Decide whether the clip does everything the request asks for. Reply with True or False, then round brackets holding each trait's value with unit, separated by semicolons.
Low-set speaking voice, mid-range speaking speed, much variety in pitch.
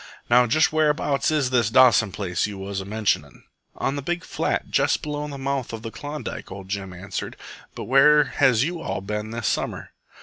True (125 Hz; 190 wpm; 6.2 semitones)